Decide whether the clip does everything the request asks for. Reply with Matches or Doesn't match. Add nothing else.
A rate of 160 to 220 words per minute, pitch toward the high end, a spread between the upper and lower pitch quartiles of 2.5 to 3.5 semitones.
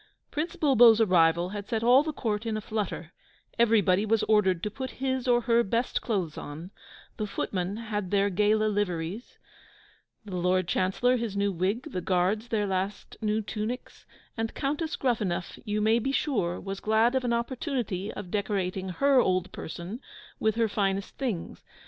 Doesn't match